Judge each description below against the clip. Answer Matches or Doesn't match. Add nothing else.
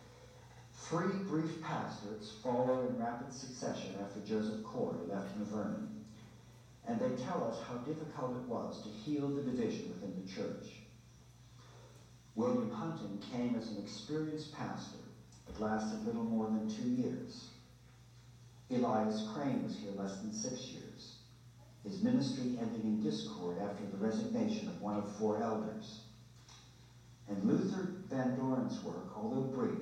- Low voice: Matches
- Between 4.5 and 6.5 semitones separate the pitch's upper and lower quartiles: Doesn't match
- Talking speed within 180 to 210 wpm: Doesn't match